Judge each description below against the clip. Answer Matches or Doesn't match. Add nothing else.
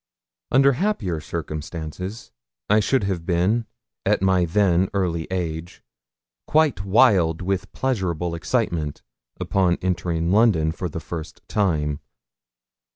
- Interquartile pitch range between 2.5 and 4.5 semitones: Matches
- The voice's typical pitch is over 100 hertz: Doesn't match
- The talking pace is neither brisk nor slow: Doesn't match